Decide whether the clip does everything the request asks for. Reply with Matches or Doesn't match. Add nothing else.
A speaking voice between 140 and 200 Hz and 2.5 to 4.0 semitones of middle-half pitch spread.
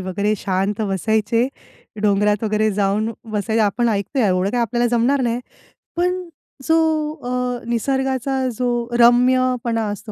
Doesn't match